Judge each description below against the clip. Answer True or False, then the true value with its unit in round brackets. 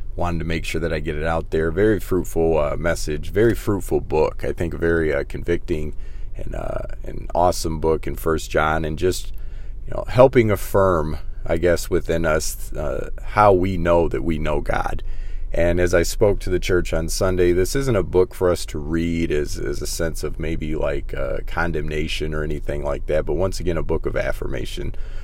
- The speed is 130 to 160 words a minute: False (205 wpm)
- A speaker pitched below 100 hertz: True (85 Hz)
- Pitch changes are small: False (3.1 semitones)